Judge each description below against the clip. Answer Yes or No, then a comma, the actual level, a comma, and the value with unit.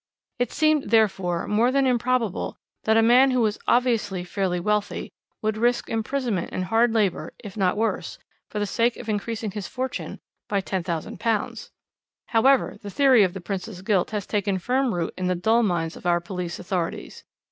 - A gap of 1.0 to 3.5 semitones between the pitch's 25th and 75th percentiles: No, average, 4.3 semitones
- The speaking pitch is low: No, high, 210 Hz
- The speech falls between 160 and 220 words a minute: Yes, average, 175 wpm